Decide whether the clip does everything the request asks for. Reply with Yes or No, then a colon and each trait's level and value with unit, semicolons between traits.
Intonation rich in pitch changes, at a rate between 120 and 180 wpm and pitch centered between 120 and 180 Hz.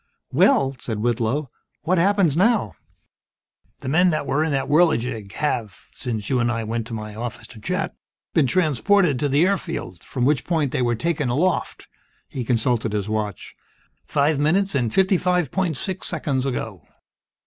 Yes: wide, 6.4 semitones; average, 170 wpm; medium, 140 Hz